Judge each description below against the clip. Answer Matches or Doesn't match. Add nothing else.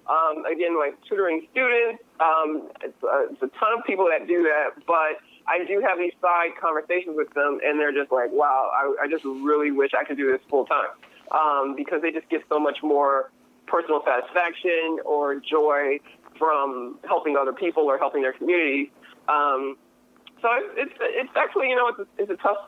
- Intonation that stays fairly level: Doesn't match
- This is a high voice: Doesn't match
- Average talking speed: Matches